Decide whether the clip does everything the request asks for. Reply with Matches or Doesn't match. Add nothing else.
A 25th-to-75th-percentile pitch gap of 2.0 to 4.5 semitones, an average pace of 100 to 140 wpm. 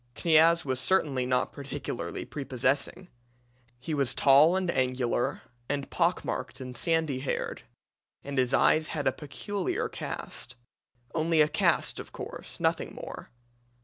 Matches